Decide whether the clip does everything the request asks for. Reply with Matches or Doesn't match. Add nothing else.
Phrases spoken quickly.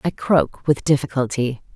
Doesn't match